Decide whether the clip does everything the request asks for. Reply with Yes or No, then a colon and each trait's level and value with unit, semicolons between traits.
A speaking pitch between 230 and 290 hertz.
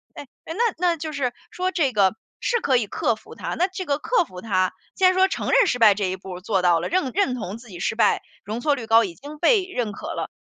Yes: very high, 250 Hz